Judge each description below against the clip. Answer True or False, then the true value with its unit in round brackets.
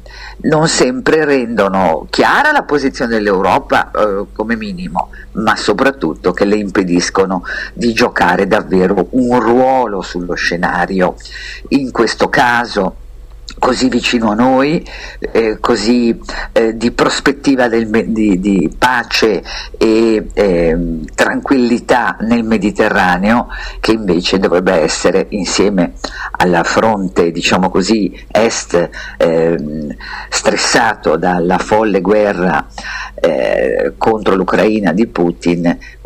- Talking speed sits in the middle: False (105 wpm)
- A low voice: True (110 Hz)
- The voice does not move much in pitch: False (5.4 semitones)